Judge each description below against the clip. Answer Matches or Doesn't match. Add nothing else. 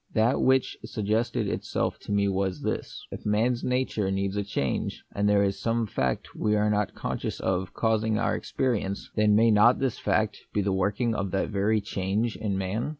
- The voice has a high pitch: Doesn't match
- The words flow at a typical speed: Matches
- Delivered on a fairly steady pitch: Matches